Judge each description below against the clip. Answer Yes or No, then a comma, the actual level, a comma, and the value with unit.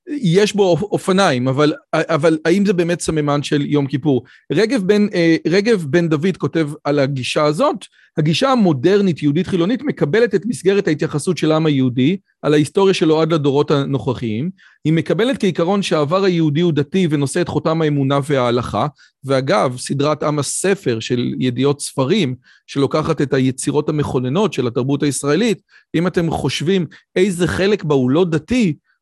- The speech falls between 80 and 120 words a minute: No, fast, 150 wpm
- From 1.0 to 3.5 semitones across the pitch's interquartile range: No, average, 4.5 semitones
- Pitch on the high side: No, medium, 160 Hz